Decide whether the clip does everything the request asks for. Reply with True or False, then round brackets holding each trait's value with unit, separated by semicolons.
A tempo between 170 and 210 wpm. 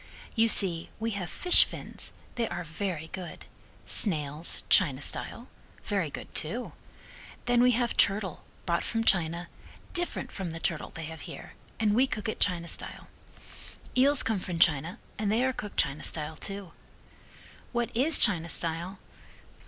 False (155 wpm)